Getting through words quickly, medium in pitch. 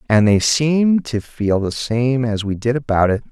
No: fast, 220 wpm; low, 120 Hz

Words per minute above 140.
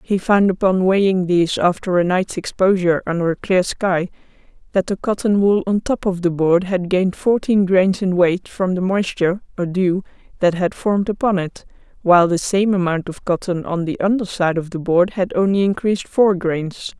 Yes: average, 200 wpm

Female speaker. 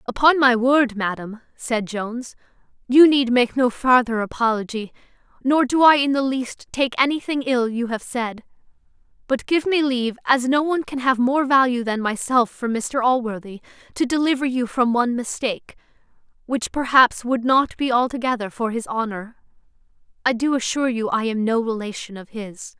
Yes: female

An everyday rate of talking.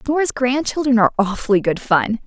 Yes: average, 160 wpm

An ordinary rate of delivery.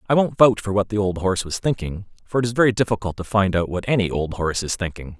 No: fast, 275 wpm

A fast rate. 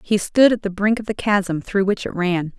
Yes: fast, 280 wpm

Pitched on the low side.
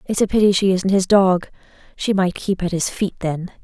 No: high, 190 Hz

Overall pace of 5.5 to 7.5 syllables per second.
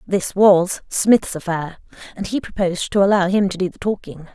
No: 5.1 syllables/s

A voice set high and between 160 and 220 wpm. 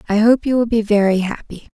No: high, 215 Hz; fast, 240 wpm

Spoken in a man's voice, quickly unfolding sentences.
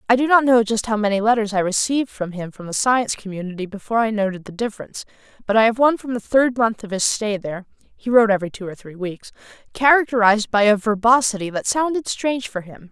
No: female; fast, 230 wpm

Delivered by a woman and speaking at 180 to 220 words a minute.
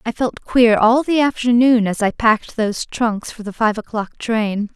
Yes: female; average, 200 wpm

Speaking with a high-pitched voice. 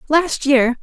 Yes: very high, 280 Hz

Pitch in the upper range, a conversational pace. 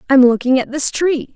No: very high, 270 Hz; fast, 220 wpm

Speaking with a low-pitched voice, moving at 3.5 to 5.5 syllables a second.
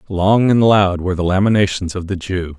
Yes: very low, 95 Hz; 5.4 syllables/s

